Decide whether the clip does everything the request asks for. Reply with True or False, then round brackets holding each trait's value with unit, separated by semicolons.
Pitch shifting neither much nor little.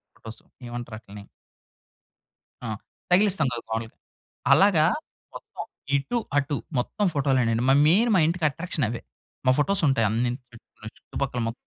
False (6.4 semitones)